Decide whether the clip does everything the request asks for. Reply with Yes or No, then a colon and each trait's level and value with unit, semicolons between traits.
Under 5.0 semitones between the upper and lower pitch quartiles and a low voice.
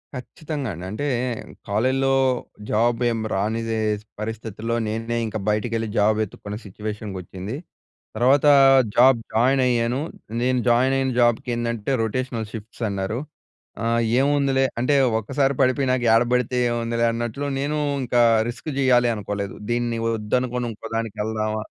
Yes: average, 2.8 semitones; low, 115 Hz